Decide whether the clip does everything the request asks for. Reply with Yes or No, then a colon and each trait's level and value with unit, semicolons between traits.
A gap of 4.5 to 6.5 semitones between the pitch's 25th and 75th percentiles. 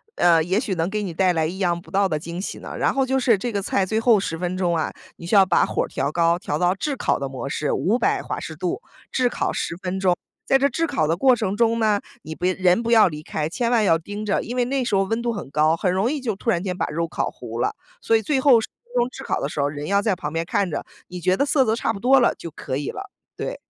Yes: wide, 5.5 semitones